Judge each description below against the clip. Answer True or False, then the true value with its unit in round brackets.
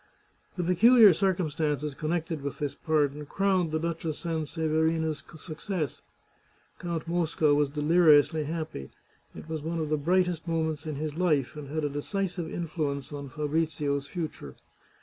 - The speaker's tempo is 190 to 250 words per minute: False (145 wpm)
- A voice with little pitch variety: True (2.3 semitones)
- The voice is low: False (155 Hz)